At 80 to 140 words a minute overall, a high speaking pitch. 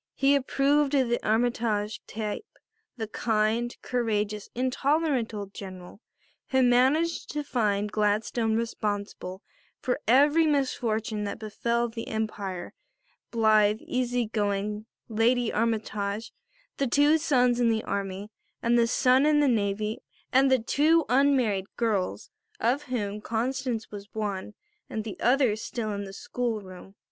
Yes: slow, 135 wpm; high, 225 Hz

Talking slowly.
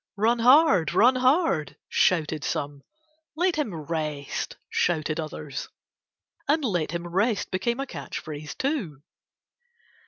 Yes: slow, 120 wpm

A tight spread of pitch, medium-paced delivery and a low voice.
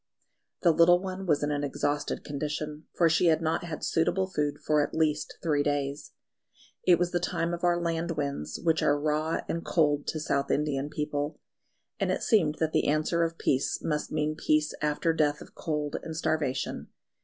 No: narrow, 2.1 semitones; average, 190 wpm; medium, 155 Hz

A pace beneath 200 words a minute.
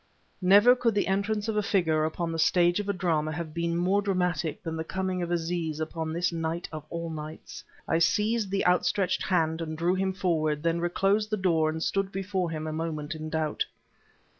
No: fast, 205 wpm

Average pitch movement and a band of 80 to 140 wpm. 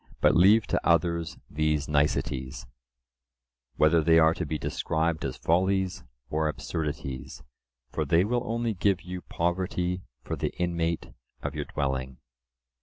Yes: average, 3.1 semitones; slow, 135 wpm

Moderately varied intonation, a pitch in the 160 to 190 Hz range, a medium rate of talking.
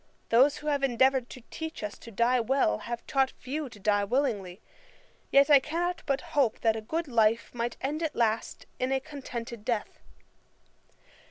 No: average, 3.7 semitones; very high, 255 Hz; average, 175 wpm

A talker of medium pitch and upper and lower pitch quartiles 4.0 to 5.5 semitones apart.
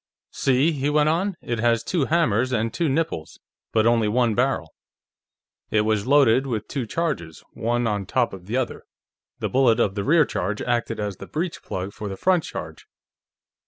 No: low, 120 Hz; average, 5.0 semitones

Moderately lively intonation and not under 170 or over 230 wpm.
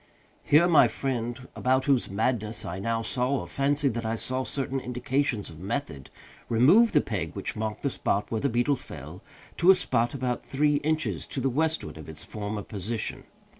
Yes: average, 4.1 semitones; average, 185 wpm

